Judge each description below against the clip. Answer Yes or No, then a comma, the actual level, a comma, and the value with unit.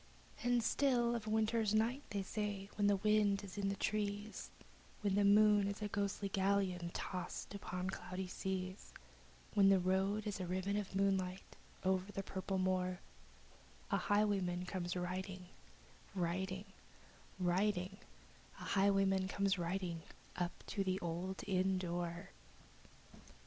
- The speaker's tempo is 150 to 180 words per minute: No, slow, 135 wpm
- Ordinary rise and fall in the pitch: No, narrow, 1.8 semitones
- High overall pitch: Yes, high, 195 Hz